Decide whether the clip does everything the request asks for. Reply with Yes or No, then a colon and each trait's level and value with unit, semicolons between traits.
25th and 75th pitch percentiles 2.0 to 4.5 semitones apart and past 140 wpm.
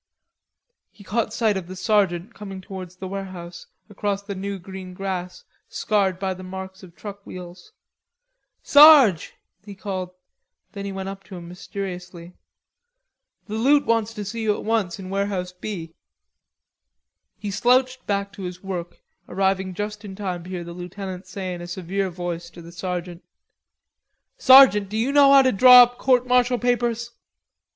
Yes: average, 3.0 semitones; average, 165 wpm